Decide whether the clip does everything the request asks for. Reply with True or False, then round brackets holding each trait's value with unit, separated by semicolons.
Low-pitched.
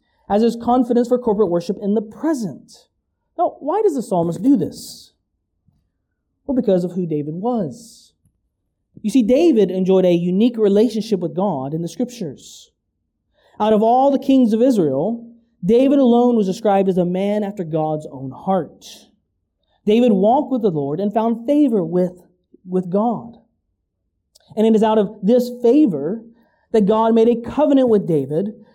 False (215 Hz)